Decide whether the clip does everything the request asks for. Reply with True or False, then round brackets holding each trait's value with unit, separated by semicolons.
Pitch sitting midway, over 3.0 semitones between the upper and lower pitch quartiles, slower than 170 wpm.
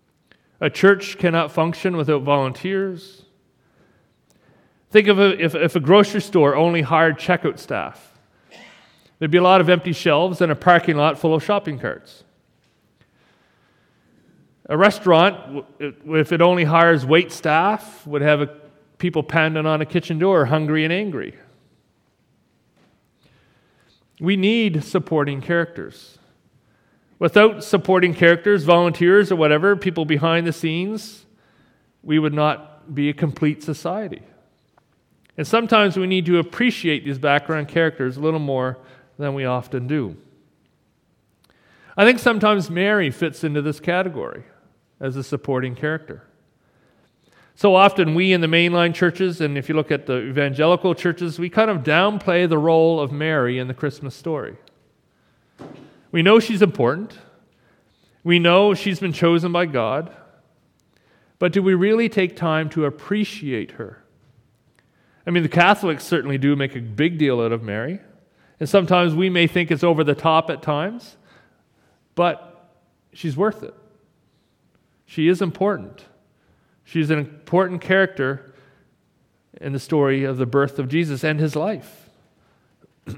True (165 Hz; 3.9 semitones; 140 wpm)